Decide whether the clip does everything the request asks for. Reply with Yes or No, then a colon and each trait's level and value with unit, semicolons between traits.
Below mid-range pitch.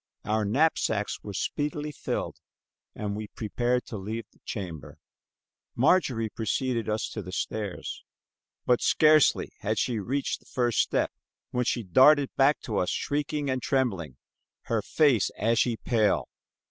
Yes: low, 115 Hz